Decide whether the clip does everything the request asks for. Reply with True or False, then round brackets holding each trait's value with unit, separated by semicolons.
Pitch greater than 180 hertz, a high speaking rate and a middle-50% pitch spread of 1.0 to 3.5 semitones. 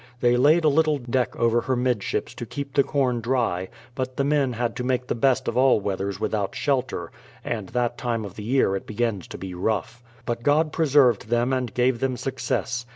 False (125 Hz; 215 wpm; 2.6 semitones)